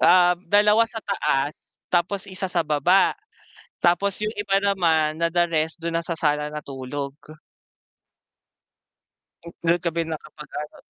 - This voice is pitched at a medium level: Yes, medium, 170 Hz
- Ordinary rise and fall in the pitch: Yes, average, 3.8 semitones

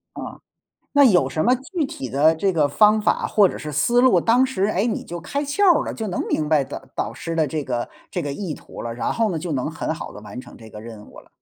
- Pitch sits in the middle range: Yes, medium, 165 Hz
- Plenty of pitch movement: Yes, wide, 8.3 semitones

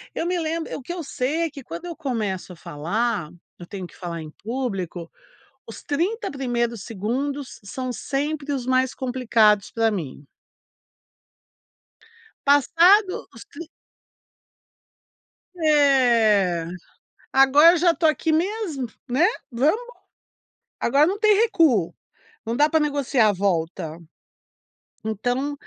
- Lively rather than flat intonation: Yes, wide, 6.5 semitones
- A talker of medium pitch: No, very high, 260 Hz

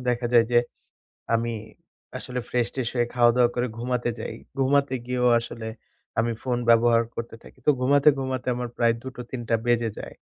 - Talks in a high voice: No, low, 120 Hz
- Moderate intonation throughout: No, narrow, 1.3 semitones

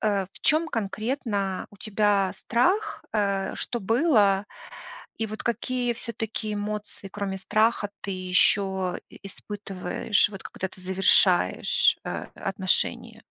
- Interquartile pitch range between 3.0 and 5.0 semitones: No, narrow, 2.6 semitones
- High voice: Yes, high, 205 Hz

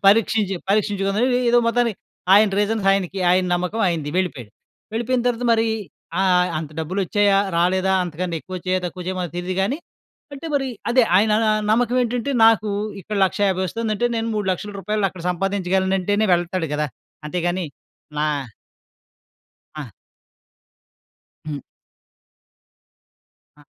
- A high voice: Yes, high, 195 Hz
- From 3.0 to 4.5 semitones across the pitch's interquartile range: Yes, average, 3.3 semitones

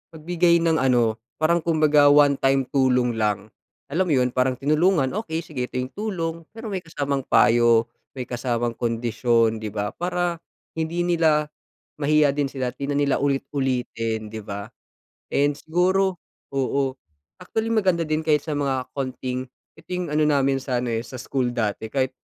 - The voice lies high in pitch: No, medium, 140 Hz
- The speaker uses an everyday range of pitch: Yes, average, 4.5 semitones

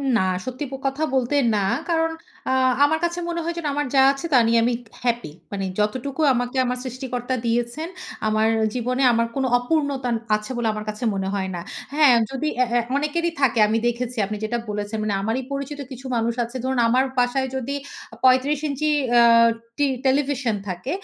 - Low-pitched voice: No, very high, 255 Hz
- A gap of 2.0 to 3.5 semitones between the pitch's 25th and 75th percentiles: Yes, average, 3.2 semitones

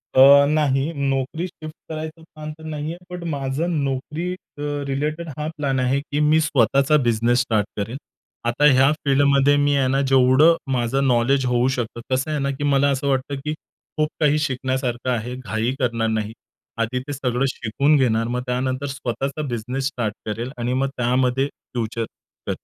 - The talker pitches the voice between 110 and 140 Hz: Yes, low, 135 Hz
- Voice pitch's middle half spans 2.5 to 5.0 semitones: Yes, average, 2.9 semitones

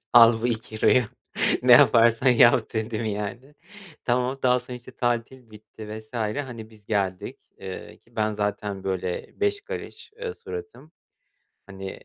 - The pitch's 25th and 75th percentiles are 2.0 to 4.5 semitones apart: Yes, average, 2.9 semitones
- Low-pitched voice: Yes, low, 115 Hz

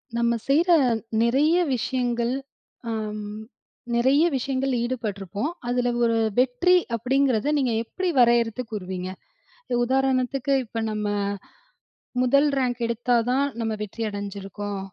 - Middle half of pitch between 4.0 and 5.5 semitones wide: No, average, 3.2 semitones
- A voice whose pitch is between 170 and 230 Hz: No, high, 245 Hz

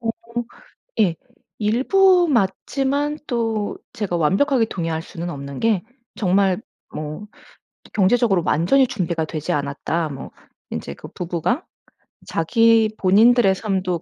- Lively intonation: Yes, wide, 5.7 semitones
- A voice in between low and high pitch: No, high, 195 Hz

